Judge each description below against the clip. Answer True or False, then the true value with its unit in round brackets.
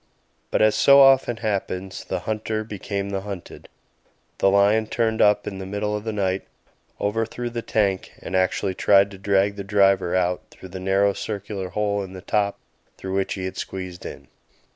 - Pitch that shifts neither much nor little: False (1.8 semitones)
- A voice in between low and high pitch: False (100 Hz)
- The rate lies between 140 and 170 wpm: False (185 wpm)